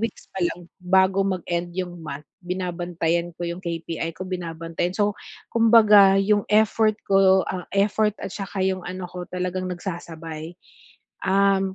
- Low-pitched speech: No, medium, 185 Hz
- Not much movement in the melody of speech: Yes, narrow, 2.2 semitones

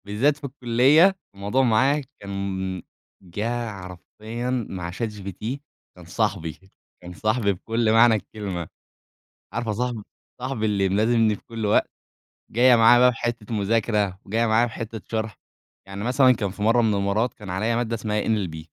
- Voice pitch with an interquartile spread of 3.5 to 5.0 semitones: No, average, 3.1 semitones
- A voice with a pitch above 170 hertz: No, low, 110 Hz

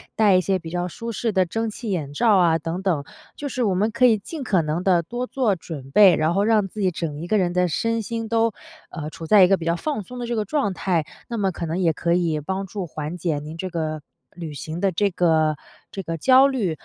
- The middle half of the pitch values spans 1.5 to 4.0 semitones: No, average, 4.9 semitones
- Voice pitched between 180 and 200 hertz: Yes, medium, 185 Hz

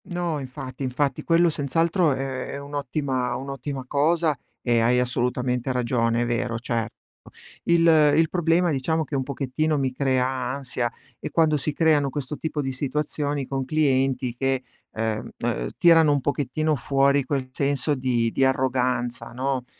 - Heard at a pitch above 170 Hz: No, low, 135 Hz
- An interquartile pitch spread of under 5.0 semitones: Yes, average, 2.9 semitones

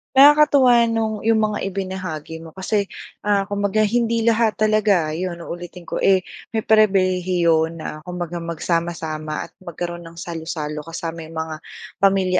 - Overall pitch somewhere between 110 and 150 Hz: No, medium, 185 Hz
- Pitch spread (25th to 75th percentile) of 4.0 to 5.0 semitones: Yes, average, 4.4 semitones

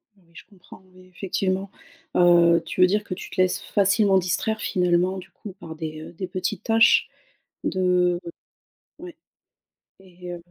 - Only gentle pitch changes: Yes, narrow, 1.7 semitones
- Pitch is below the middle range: No, medium, 185 Hz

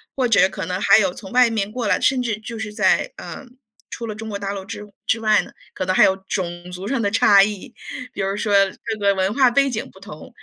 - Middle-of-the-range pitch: No, high, 210 Hz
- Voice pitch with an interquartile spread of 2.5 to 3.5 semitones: Yes, average, 2.9 semitones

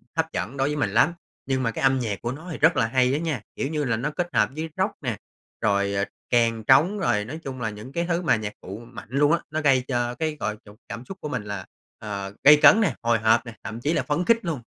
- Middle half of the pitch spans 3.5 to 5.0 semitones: No, wide, 5.6 semitones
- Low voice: Yes, low, 130 Hz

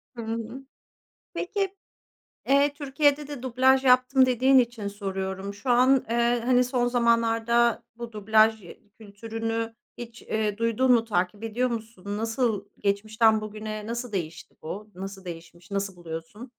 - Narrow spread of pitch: No, average, 3.4 semitones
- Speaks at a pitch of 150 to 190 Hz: No, high, 225 Hz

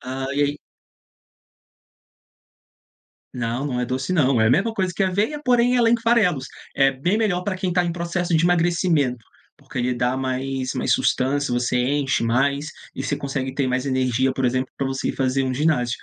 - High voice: No, low, 135 Hz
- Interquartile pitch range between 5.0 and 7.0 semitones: Yes, wide, 5.5 semitones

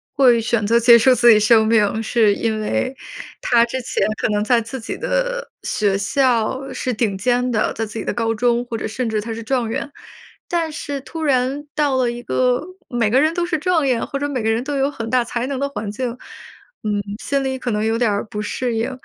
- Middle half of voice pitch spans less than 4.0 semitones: Yes, average, 3.2 semitones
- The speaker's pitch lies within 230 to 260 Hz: Yes, high, 240 Hz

